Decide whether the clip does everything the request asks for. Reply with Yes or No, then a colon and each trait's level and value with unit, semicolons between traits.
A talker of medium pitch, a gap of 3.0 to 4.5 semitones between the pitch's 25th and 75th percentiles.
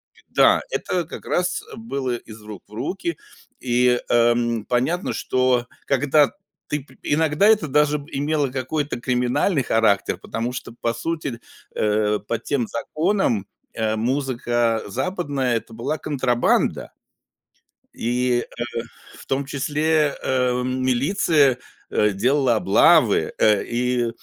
No: low, 125 Hz; average, 3.9 semitones